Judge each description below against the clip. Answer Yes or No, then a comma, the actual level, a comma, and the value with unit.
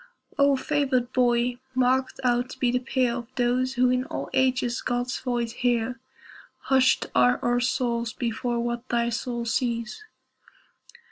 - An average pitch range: No, narrow, 1.3 semitones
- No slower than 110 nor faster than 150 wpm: Yes, average, 145 wpm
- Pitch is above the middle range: Yes, high, 245 Hz